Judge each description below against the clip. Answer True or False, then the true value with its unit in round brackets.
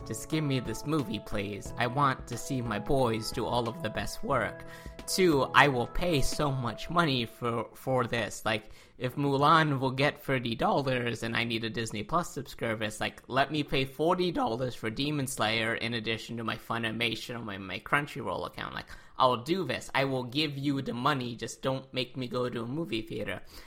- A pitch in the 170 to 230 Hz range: False (125 Hz)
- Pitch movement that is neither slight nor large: True (3.9 semitones)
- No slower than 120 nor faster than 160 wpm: False (205 wpm)